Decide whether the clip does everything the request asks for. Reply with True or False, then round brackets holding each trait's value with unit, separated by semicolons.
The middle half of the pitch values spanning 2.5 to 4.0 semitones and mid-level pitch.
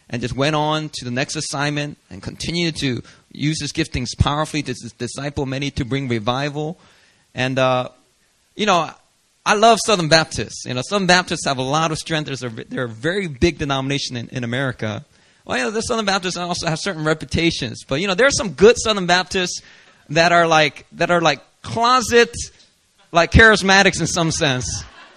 False (4.8 semitones; 155 Hz)